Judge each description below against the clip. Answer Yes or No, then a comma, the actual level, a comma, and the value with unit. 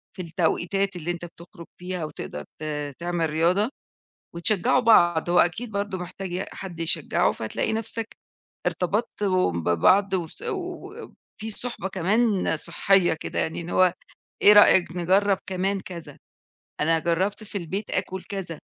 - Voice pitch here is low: No, medium, 185 Hz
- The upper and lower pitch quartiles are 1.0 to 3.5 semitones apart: Yes, average, 3.0 semitones